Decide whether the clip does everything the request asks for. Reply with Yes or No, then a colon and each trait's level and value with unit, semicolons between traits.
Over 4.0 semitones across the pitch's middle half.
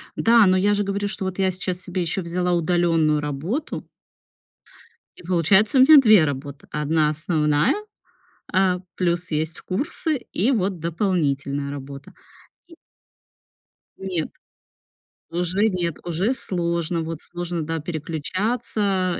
No: average, 3.5 semitones